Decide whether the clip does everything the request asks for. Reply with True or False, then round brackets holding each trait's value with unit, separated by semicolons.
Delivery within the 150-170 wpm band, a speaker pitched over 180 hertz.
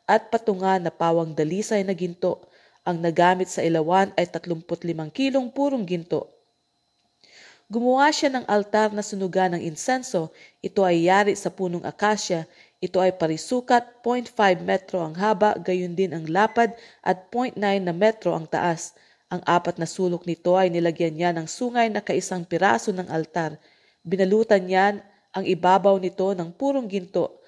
True (155 wpm; 190 Hz)